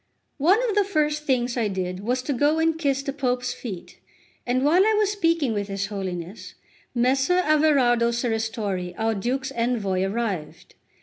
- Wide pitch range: Yes, wide, 6.3 semitones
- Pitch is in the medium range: No, high, 245 Hz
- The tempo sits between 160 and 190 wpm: Yes, average, 170 wpm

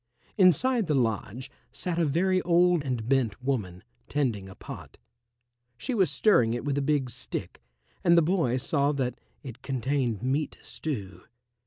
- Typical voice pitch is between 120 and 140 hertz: Yes, low, 135 Hz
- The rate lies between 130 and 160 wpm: Yes, average, 155 wpm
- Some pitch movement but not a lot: No, wide, 5.8 semitones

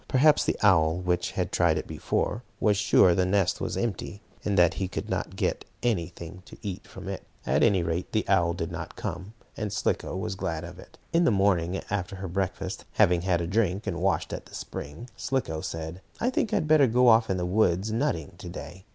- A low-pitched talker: Yes, very low, 95 Hz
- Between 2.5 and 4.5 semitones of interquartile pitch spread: Yes, average, 3.5 semitones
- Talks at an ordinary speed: No, fast, 220 wpm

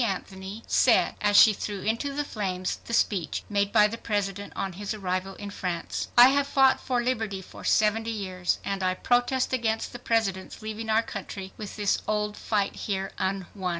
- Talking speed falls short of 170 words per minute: No, average, 185 wpm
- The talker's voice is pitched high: Yes, high, 205 Hz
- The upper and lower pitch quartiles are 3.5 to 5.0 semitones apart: No, average, 2.7 semitones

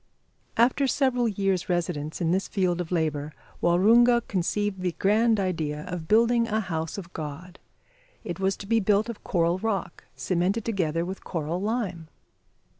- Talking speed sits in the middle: Yes, average, 155 wpm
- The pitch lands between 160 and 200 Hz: Yes, medium, 185 Hz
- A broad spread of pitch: No, average, 4.3 semitones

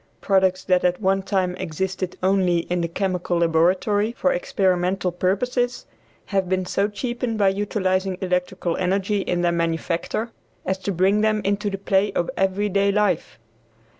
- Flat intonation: Yes, narrow, 2.1 semitones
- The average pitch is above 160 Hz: Yes, high, 190 Hz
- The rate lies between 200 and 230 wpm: No, average, 155 wpm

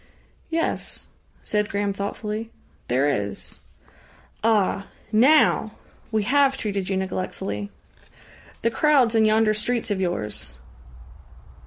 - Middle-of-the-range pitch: No, high, 210 Hz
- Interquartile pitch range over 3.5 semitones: No, average, 3.2 semitones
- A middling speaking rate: No, slow, 105 wpm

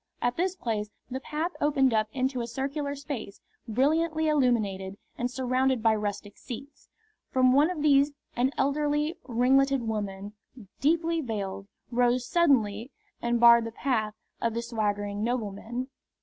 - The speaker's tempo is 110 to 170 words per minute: Yes, average, 140 wpm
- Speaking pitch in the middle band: No, very high, 250 Hz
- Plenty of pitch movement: No, average, 4.3 semitones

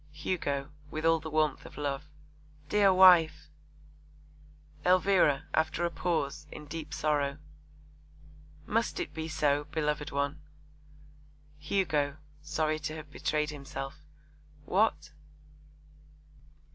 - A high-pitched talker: No, medium, 155 Hz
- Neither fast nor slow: No, slow, 105 wpm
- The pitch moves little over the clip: Yes, narrow, 2.1 semitones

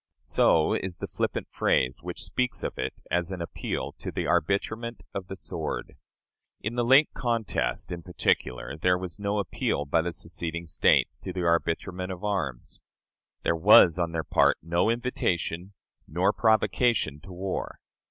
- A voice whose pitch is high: No, very low, 90 Hz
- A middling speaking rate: Yes, average, 160 wpm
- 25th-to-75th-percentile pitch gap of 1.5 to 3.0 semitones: No, average, 3.6 semitones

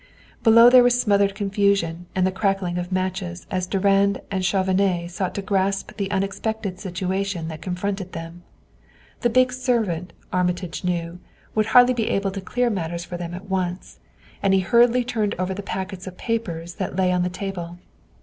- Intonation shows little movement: Yes, narrow, 2.2 semitones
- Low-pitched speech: No, high, 190 Hz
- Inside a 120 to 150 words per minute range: No, average, 175 wpm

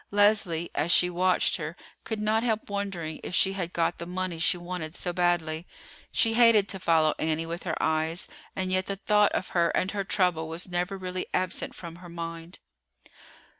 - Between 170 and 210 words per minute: Yes, average, 190 wpm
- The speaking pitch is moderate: Yes, medium, 180 Hz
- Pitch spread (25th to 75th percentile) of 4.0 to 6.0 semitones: No, narrow, 2.6 semitones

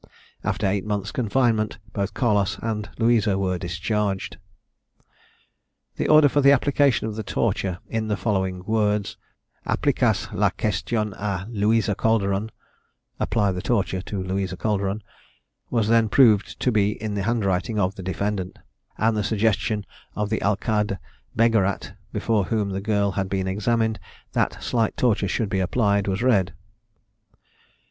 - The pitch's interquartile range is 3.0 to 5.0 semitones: No, narrow, 2.4 semitones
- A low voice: Yes, low, 105 Hz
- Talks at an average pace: Yes, average, 145 wpm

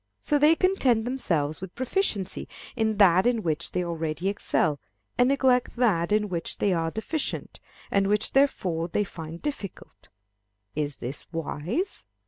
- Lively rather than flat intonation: Yes, wide, 7.0 semitones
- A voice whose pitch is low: No, high, 200 Hz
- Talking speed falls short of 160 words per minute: Yes, average, 145 wpm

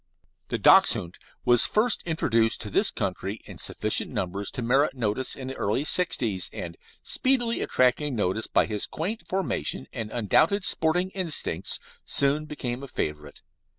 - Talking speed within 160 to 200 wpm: No, average, 150 wpm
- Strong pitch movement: Yes, wide, 7.6 semitones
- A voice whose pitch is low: Yes, low, 125 Hz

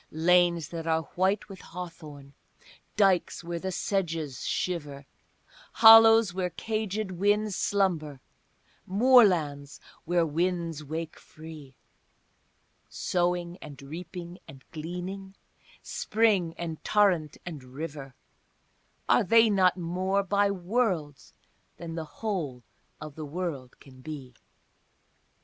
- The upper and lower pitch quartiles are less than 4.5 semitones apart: Yes, average, 3.9 semitones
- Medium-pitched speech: Yes, medium, 175 Hz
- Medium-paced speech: No, slow, 105 wpm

